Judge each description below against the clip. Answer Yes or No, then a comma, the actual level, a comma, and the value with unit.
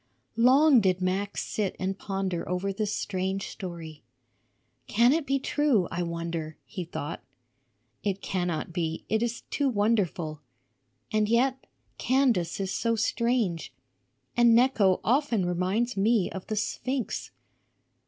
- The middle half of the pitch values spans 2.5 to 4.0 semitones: No, average, 4.8 semitones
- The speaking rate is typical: No, slow, 130 wpm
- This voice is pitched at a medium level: No, high, 200 Hz